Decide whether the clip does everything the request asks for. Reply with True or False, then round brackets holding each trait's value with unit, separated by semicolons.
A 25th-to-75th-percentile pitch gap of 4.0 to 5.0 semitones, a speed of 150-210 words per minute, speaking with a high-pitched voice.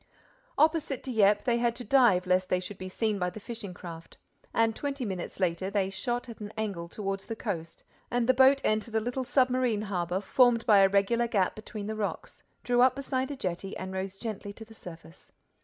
True (4.3 semitones; 205 wpm; 215 Hz)